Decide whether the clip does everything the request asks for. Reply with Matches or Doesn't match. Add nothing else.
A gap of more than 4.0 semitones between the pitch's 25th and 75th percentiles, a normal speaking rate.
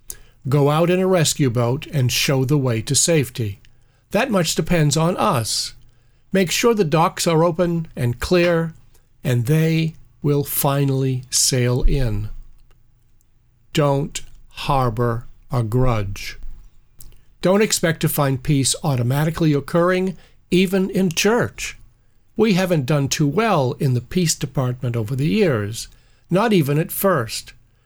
Doesn't match